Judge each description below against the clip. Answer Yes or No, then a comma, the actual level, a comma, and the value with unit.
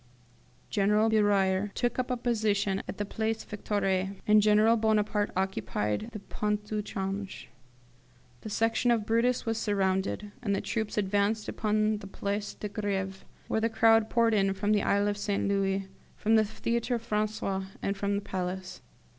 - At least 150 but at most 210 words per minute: Yes, average, 160 wpm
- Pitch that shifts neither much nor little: No, narrow, 1.9 semitones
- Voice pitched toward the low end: No, high, 210 Hz